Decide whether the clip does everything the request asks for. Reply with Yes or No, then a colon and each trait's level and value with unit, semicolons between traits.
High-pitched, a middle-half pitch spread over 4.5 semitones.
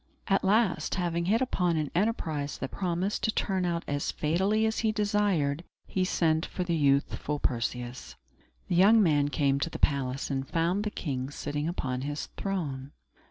No: medium, 165 Hz; average, 5.3 semitones